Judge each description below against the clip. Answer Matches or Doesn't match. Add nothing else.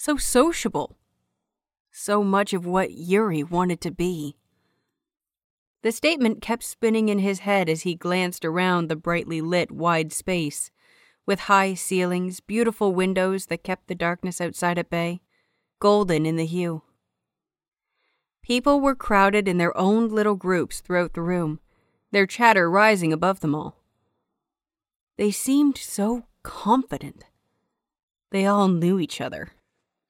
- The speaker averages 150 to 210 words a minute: Doesn't match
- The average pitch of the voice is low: Doesn't match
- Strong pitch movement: Doesn't match